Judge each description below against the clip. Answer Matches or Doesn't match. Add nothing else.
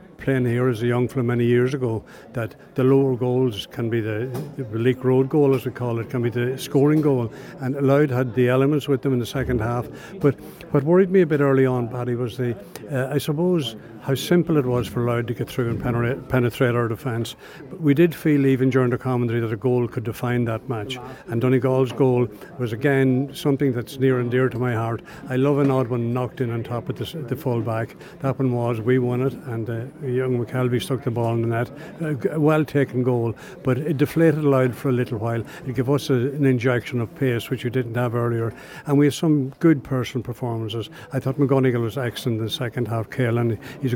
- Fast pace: Matches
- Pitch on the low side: Matches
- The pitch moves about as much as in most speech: Doesn't match